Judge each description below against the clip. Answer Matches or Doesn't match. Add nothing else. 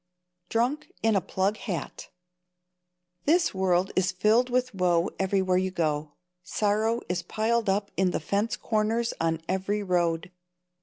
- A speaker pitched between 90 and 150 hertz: Doesn't match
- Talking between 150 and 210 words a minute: Doesn't match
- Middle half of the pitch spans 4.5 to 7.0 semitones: Doesn't match